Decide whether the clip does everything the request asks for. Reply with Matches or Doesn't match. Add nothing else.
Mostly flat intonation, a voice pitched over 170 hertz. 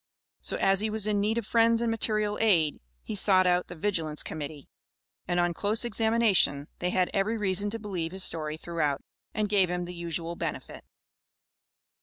Doesn't match